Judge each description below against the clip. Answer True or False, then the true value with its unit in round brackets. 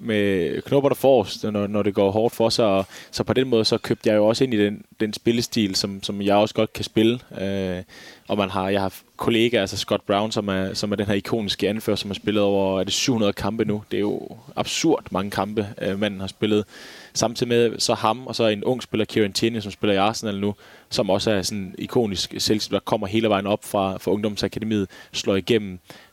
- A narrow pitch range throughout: True (2.1 semitones)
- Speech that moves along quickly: True (230 wpm)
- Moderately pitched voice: False (105 Hz)